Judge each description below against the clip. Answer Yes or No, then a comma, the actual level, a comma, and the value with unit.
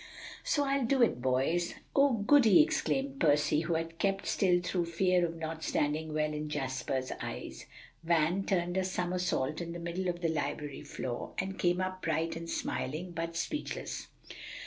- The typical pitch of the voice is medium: Yes, medium, 170 Hz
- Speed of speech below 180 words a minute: Yes, average, 170 wpm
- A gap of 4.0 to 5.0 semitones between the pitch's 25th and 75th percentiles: No, average, 3.2 semitones